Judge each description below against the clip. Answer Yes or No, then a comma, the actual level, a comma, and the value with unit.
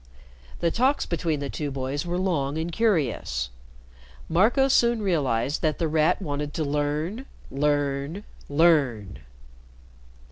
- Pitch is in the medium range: Yes, medium, 155 Hz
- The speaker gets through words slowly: Yes, slow, 120 wpm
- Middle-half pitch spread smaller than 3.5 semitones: No, average, 3.9 semitones